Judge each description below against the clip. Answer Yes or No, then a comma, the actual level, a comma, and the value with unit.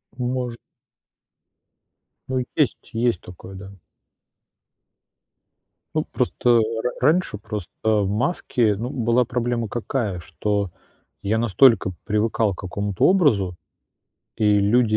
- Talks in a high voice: No, low, 110 Hz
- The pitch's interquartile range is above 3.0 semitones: Yes, average, 3.4 semitones